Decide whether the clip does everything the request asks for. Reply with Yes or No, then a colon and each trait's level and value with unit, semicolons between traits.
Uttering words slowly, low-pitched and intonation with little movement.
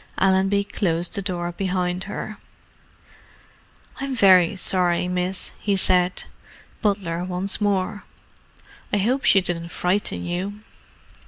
No: slow, 105 wpm; high, 190 Hz; narrow, 2.1 semitones